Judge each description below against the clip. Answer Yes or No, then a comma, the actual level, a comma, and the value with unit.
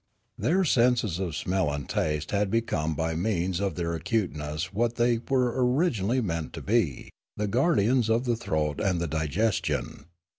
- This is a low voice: Yes, low, 100 Hz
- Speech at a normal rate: Yes, average, 160 wpm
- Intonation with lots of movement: Yes, wide, 6.5 semitones